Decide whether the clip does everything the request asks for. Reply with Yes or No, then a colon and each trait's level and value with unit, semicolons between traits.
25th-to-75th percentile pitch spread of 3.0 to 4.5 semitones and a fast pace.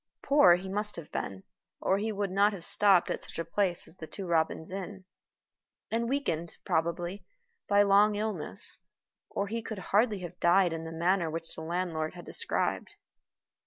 No: average, 3.5 semitones; average, 175 wpm